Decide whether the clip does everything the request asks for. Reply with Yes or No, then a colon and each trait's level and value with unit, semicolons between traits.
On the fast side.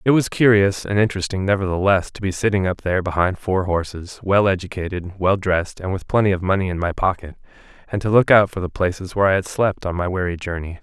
Yes: fast, 225 wpm